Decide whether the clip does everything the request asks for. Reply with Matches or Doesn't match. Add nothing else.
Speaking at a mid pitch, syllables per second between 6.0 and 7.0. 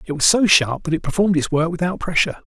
Matches